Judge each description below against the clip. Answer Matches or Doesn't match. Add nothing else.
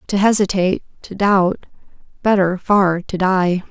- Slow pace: Matches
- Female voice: Matches